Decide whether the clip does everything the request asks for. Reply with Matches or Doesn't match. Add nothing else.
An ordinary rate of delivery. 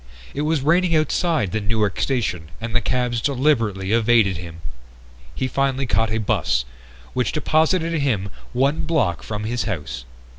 Matches